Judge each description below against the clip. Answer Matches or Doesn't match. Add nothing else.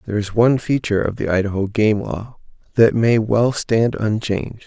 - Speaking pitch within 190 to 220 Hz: Doesn't match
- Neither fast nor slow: Matches